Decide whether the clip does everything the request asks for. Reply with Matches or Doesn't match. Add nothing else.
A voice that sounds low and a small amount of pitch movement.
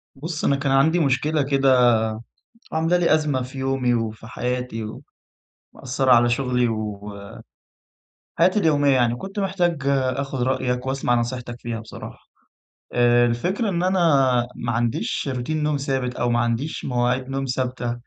Doesn't match